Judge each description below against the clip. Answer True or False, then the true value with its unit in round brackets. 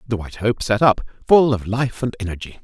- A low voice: True (110 Hz)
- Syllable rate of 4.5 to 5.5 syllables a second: False (5.8 syllables/s)